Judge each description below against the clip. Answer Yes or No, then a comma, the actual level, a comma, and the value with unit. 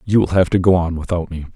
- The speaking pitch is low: Yes, very low, 90 Hz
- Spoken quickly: Yes, fast, 310 wpm